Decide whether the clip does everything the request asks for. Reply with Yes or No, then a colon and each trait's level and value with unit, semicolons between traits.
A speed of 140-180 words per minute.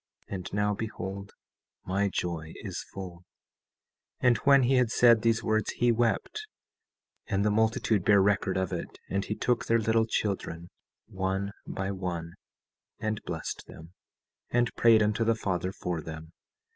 Yes: average, 155 wpm